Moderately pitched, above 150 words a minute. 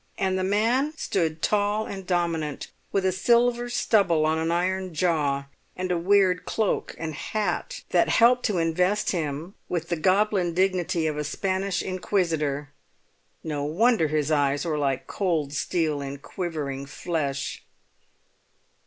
No: medium, 175 Hz; average, 145 wpm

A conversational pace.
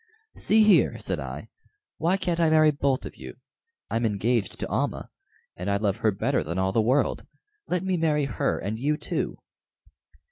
Yes: average, 180 wpm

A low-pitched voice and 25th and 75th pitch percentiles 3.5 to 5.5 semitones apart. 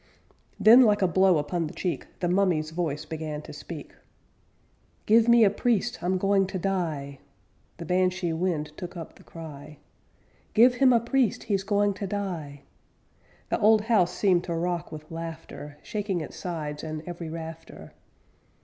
No: medium, 180 Hz; average, 4.0 semitones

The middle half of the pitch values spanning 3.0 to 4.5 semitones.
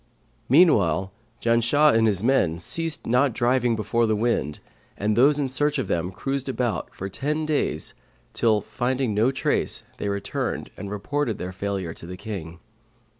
No: average, 5.3 semitones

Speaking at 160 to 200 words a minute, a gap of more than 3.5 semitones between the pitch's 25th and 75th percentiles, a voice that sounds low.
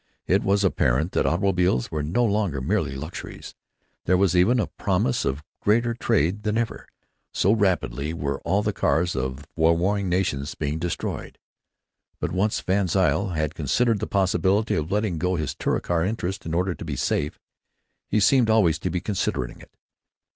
Yes: average, 170 wpm; average, 4.6 semitones; very low, 90 Hz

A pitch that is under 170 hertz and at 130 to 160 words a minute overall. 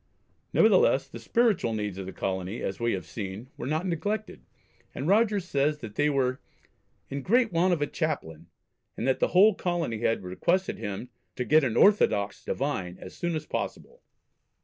No: medium, 140 Hz; average, 175 wpm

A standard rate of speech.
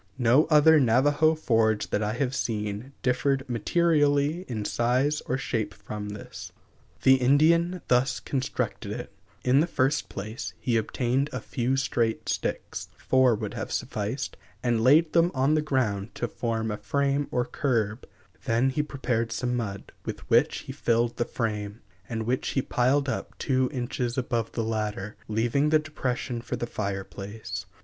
Yes: average, 160 wpm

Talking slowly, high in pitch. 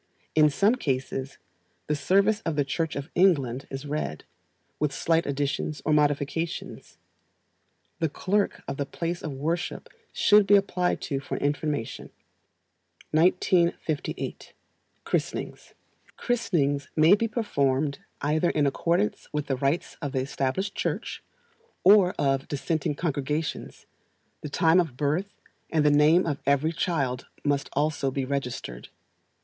No: slow, 130 wpm; medium, 150 Hz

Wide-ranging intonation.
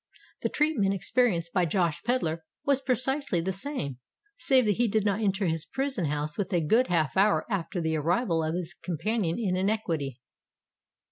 Yes: wide, 5.9 semitones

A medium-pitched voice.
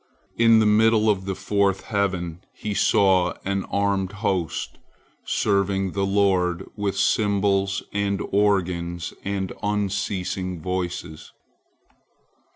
No: low, 100 Hz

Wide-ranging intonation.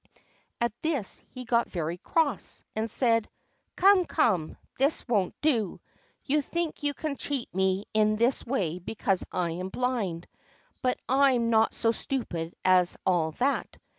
Yes: wide, 6.4 semitones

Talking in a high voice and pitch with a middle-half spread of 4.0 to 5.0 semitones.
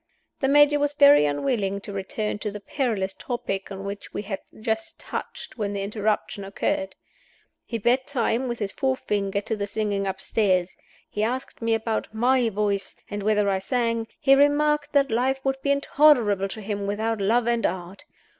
Yes: high, 220 Hz; average, 4.4 semitones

